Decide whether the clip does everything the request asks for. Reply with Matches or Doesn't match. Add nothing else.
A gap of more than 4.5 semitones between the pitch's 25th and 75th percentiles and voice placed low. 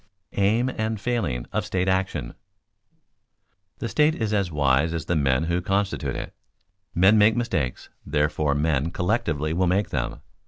Matches